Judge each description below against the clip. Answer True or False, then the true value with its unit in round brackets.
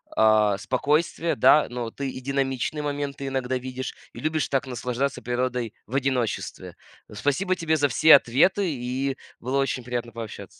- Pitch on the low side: True (130 Hz)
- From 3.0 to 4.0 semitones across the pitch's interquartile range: False (2.5 semitones)